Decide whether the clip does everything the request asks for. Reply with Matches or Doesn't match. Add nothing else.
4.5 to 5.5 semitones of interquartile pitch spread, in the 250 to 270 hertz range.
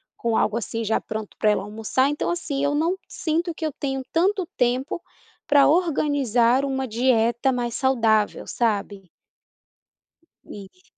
Matches